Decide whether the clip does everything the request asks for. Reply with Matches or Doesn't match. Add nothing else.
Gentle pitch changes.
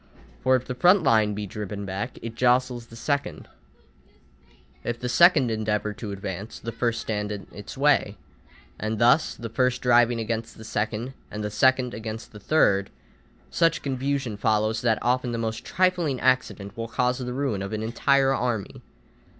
Doesn't match